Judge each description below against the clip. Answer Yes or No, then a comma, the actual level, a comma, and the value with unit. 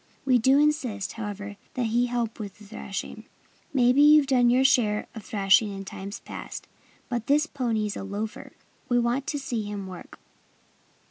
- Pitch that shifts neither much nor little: Yes, average, 3.9 semitones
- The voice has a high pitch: Yes, high, 230 Hz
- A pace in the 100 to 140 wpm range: No, average, 175 wpm